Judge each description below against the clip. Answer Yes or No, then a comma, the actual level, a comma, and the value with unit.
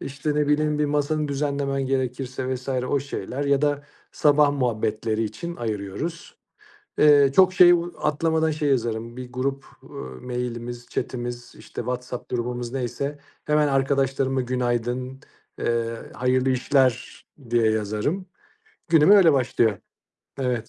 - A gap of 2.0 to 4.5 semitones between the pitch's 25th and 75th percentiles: Yes, average, 3.2 semitones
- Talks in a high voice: No, low, 130 Hz